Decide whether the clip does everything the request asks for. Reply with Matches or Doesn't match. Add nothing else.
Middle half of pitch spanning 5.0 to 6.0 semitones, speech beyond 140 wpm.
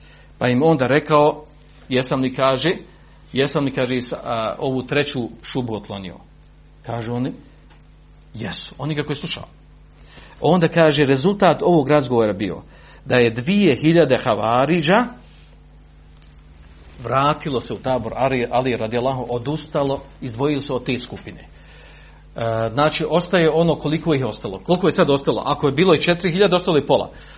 Matches